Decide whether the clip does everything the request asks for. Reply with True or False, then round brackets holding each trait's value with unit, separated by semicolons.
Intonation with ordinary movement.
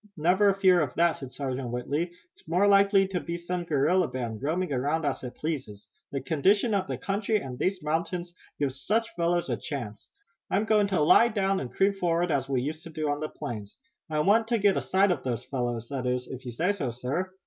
False (6.4 semitones)